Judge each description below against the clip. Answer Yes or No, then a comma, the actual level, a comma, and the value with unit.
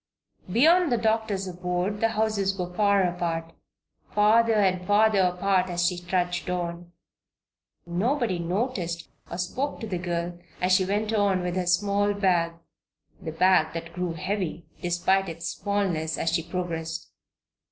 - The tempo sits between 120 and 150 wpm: Yes, average, 145 wpm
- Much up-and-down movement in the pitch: No, average, 2.8 semitones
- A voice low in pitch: No, medium, 185 Hz